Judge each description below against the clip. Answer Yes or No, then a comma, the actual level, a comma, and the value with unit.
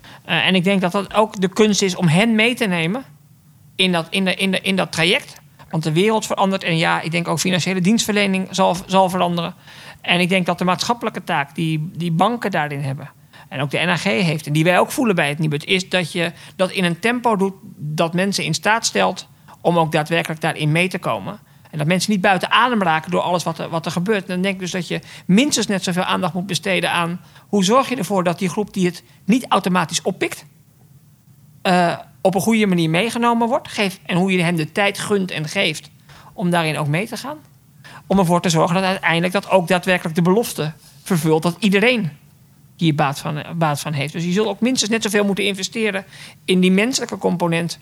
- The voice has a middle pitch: Yes, medium, 180 Hz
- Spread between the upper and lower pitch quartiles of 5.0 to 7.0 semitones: No, average, 3.9 semitones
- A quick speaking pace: Yes, fast, 225 wpm